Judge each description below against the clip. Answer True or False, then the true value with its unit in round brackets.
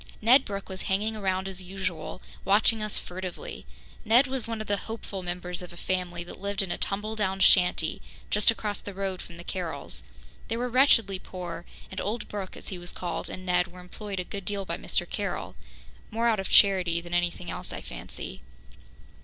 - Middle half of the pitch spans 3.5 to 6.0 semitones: False (2.8 semitones)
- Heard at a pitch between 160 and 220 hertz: True (190 Hz)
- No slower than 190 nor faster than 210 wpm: True (200 wpm)